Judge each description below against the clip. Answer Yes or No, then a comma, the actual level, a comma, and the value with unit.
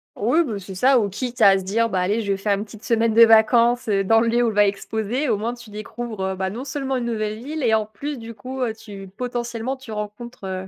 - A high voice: Yes, high, 225 Hz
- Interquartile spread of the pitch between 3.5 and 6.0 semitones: No, average, 2.9 semitones